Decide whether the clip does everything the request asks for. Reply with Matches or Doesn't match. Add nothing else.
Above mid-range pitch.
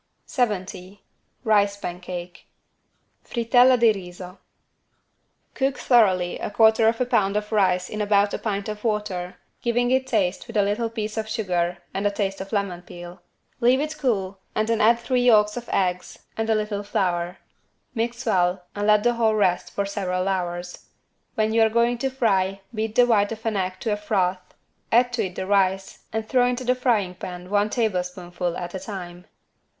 Matches